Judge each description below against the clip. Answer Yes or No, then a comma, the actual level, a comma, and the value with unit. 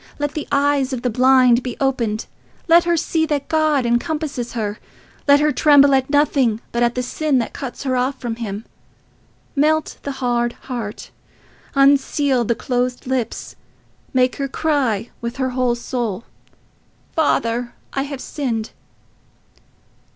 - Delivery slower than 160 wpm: Yes, average, 145 wpm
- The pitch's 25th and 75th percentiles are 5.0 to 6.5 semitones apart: No, average, 3.1 semitones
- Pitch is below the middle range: No, very high, 260 Hz